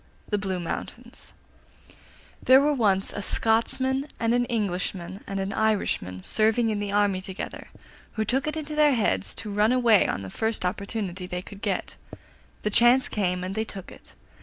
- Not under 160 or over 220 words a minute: Yes, average, 175 wpm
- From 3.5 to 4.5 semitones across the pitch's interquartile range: Yes, average, 3.9 semitones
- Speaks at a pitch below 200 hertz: No, high, 210 Hz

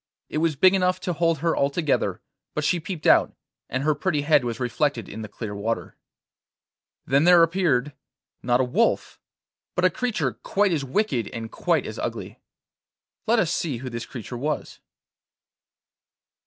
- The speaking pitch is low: No, medium, 150 Hz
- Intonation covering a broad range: Yes, wide, 5.8 semitones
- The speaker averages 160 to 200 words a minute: Yes, average, 165 wpm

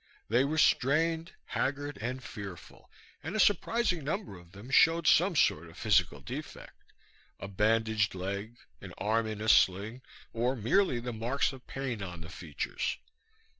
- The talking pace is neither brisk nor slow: Yes, average, 155 wpm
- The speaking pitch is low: Yes, low, 115 Hz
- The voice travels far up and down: Yes, wide, 6.4 semitones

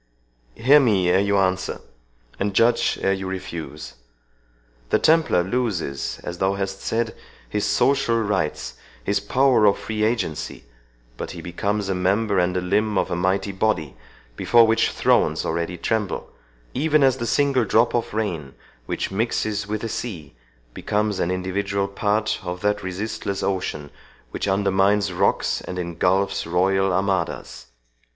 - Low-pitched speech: Yes, low, 100 Hz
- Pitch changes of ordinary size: Yes, average, 3.3 semitones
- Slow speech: No, average, 145 wpm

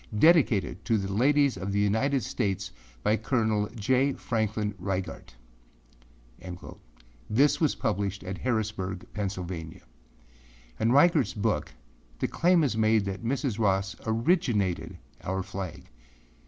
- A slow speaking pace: Yes, slow, 115 wpm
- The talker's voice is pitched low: Yes, low, 105 Hz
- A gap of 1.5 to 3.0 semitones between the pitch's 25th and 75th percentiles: No, average, 4.2 semitones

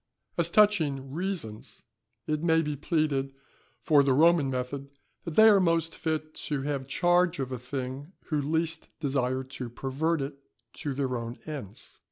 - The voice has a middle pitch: Yes, medium, 145 Hz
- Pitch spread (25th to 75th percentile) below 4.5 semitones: Yes, average, 3.6 semitones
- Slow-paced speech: No, average, 160 wpm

